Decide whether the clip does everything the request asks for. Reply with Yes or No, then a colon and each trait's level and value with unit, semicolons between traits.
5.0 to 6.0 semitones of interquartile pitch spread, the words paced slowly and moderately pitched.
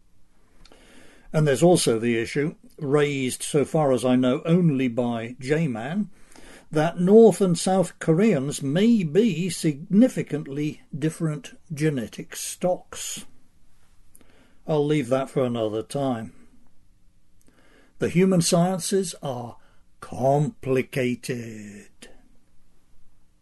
Yes: wide, 5.4 semitones; slow, 95 wpm; medium, 150 Hz